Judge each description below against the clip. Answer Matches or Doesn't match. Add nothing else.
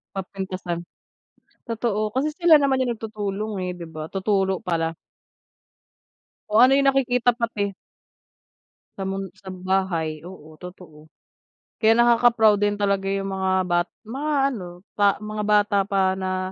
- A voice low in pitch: Doesn't match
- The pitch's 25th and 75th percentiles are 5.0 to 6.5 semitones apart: Doesn't match